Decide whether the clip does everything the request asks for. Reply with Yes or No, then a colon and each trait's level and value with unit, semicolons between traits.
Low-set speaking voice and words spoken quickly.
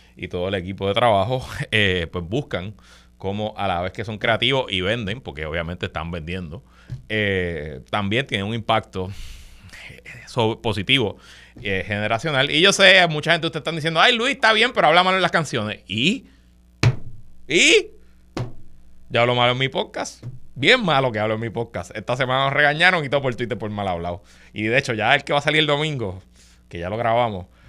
Yes: low, 115 Hz; fast, 195 wpm